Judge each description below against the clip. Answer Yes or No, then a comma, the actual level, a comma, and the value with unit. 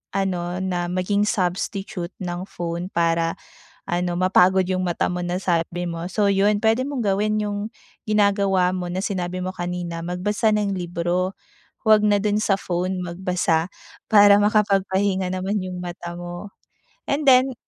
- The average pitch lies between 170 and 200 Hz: Yes, medium, 185 Hz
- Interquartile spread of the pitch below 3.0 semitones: Yes, narrow, 2.6 semitones